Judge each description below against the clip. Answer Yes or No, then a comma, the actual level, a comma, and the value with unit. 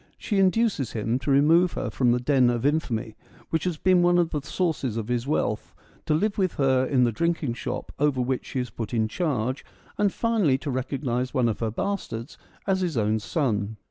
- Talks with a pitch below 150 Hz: Yes, low, 135 Hz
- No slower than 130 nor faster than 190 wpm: No, fast, 205 wpm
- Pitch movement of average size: No, wide, 6.0 semitones